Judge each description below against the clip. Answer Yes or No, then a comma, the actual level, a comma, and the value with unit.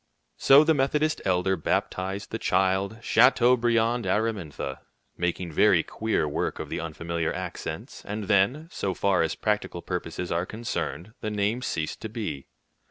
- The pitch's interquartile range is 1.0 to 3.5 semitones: No, average, 4.7 semitones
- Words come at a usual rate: Yes, average, 145 wpm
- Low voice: Yes, low, 100 Hz